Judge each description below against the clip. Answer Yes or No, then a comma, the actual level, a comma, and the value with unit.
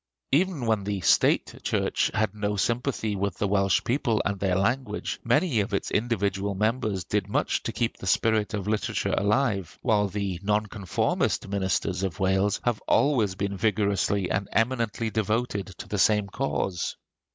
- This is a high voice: No, low, 105 Hz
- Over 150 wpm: Yes, average, 160 wpm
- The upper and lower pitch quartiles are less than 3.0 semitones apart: Yes, narrow, 2.4 semitones